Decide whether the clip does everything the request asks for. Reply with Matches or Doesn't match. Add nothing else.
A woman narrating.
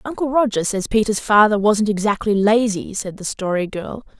Matches